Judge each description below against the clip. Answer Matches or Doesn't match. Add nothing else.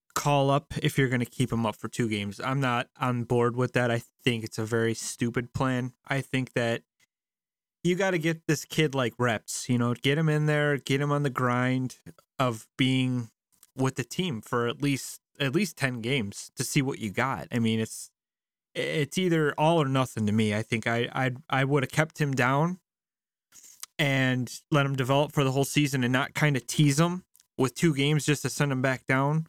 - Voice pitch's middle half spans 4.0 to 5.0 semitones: Doesn't match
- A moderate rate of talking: Doesn't match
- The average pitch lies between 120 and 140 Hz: Matches